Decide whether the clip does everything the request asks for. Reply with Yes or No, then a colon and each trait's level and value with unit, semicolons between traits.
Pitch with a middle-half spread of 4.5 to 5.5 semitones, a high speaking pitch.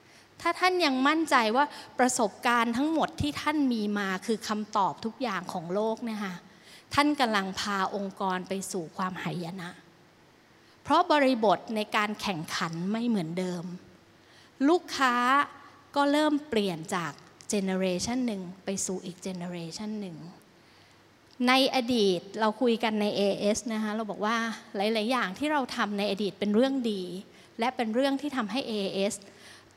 Yes: average, 5.0 semitones; high, 215 Hz